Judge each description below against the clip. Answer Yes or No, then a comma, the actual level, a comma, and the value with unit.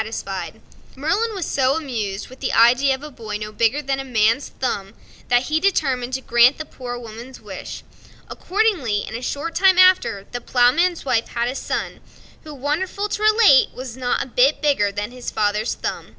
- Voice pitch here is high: Yes, very high, 260 Hz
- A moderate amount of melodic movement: Yes, average, 4.7 semitones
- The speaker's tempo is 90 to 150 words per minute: No, average, 190 wpm